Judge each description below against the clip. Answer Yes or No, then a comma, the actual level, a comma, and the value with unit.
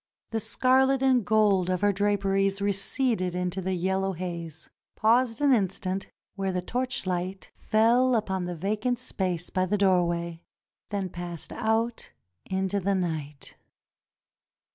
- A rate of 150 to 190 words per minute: No, average, 140 wpm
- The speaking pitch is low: No, high, 195 Hz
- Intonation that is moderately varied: Yes, average, 3.3 semitones